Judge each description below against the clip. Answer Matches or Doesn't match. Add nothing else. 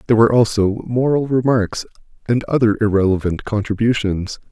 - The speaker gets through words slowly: Matches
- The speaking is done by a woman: Doesn't match